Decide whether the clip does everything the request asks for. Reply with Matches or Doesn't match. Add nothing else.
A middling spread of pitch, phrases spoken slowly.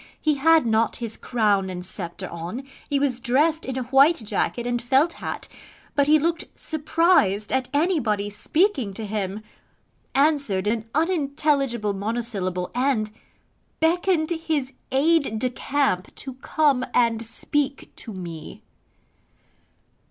Doesn't match